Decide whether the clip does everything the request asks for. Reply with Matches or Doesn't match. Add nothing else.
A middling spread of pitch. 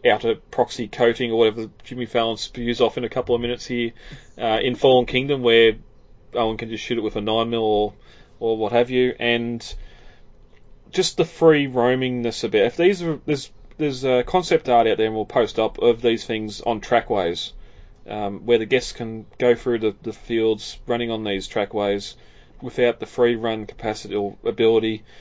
Doesn't match